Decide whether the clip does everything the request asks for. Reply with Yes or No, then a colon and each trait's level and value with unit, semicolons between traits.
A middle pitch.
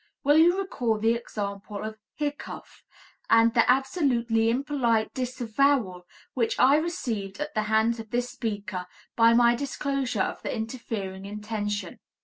No: high, 230 Hz